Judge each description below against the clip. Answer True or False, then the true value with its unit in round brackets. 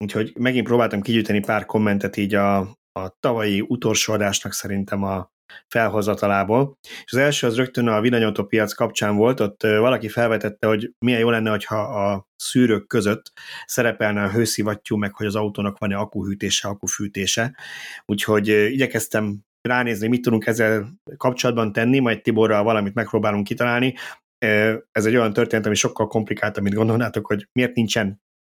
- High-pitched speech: False (110 Hz)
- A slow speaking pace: False (150 wpm)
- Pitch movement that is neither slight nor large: False (2.2 semitones)